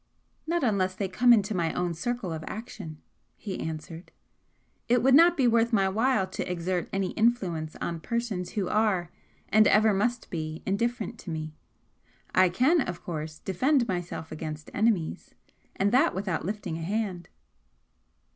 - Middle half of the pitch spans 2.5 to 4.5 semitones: No, average, 5.3 semitones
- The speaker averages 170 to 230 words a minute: No, average, 155 wpm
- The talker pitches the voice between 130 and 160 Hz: No, high, 195 Hz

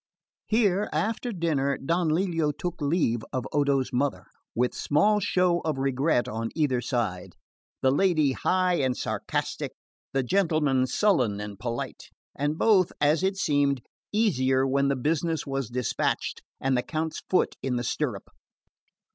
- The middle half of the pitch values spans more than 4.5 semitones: Yes, average, 5.0 semitones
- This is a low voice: No, medium, 145 Hz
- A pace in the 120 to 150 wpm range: Yes, average, 145 wpm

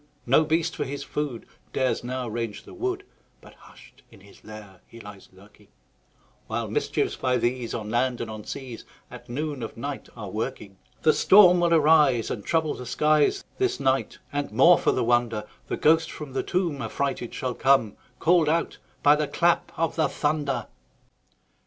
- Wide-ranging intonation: No, average, 5.0 semitones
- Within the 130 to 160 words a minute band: No, average, 180 wpm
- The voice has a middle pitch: No, low, 130 Hz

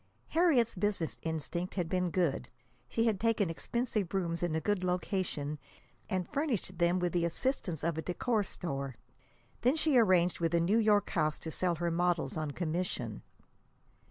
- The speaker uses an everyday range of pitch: Yes, average, 4.0 semitones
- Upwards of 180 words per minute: No, average, 165 wpm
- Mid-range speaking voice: Yes, medium, 180 Hz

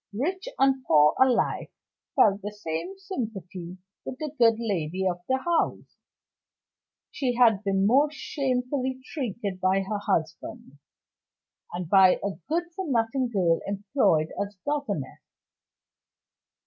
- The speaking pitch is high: Yes, high, 220 Hz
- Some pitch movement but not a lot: No, wide, 6.0 semitones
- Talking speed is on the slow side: Yes, slow, 120 wpm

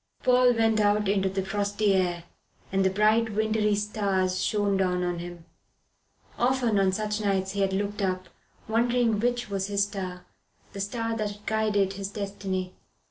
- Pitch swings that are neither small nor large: No, narrow, 2.1 semitones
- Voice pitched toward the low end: No, high, 205 Hz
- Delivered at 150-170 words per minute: Yes, average, 160 wpm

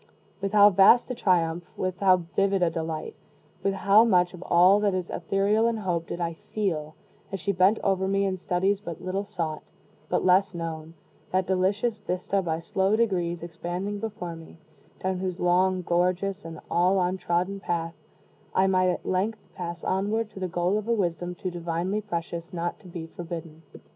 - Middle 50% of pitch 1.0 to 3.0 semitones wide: Yes, narrow, 2.4 semitones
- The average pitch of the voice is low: No, medium, 185 Hz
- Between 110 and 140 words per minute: No, average, 180 wpm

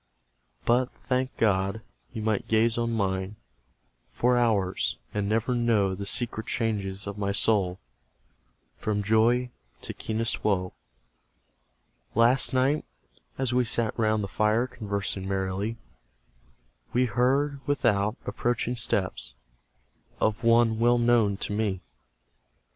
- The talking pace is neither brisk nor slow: No, slow, 120 wpm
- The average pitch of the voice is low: Yes, low, 110 Hz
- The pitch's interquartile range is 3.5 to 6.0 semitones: No, average, 3.1 semitones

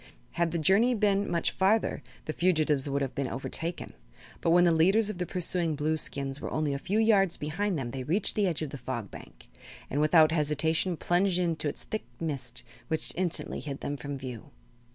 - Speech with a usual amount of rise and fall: Yes, average, 4.4 semitones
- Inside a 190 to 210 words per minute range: Yes, average, 195 wpm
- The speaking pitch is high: No, medium, 160 Hz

